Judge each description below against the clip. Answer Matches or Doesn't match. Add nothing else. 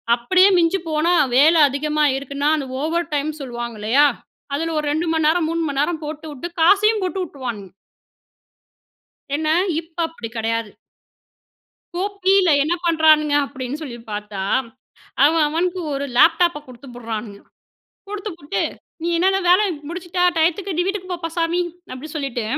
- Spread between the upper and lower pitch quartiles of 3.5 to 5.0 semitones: Matches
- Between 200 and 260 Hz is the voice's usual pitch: Doesn't match